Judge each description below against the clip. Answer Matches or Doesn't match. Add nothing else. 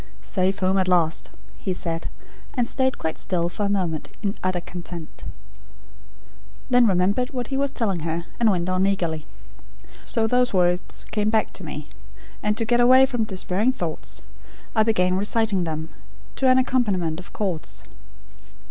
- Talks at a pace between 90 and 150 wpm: Doesn't match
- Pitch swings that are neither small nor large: Matches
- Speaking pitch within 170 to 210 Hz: Matches